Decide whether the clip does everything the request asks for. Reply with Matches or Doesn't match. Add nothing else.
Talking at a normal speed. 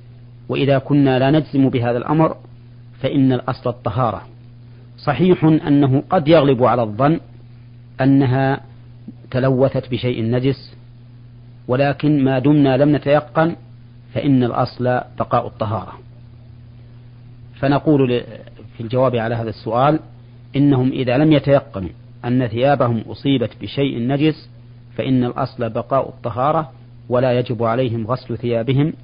Matches